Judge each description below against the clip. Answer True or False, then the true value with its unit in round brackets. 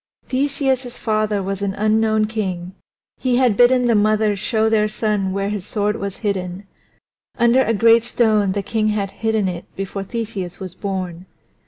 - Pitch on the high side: True (215 Hz)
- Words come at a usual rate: True (165 wpm)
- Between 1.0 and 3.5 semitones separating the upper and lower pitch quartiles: True (2.6 semitones)